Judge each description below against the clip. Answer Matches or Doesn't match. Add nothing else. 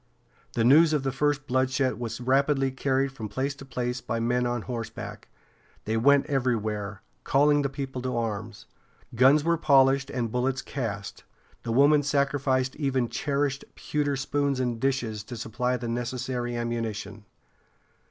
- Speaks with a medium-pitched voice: Doesn't match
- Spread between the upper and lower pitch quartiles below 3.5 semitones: Matches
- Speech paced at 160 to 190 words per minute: Doesn't match